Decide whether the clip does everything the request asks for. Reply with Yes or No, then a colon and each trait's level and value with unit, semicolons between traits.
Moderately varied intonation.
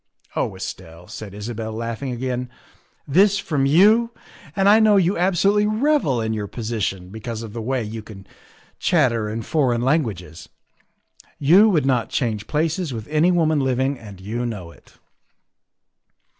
No: wide, 7.3 semitones